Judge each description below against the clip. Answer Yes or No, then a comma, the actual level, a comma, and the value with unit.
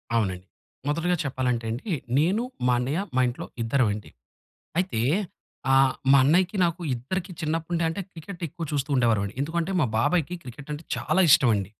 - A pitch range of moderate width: No, wide, 5.7 semitones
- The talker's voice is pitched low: No, medium, 145 Hz